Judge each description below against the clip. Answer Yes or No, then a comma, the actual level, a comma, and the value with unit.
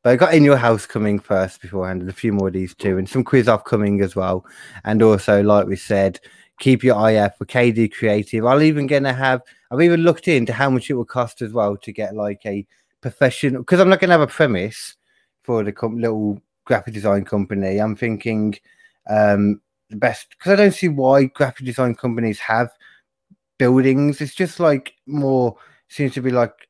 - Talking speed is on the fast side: Yes, fast, 210 wpm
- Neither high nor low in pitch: No, low, 120 Hz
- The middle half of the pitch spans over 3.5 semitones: Yes, average, 4.8 semitones